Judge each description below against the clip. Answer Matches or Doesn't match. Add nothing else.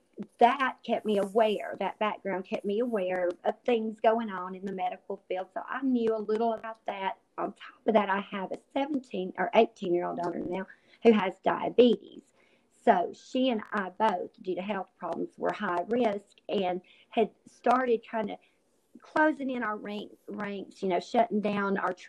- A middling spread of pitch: Matches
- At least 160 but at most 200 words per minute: Matches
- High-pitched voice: Matches